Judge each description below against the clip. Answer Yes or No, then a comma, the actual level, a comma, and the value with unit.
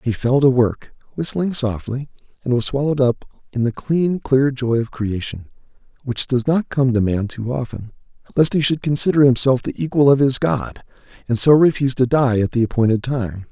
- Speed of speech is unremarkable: Yes, average, 195 wpm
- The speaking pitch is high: No, low, 130 Hz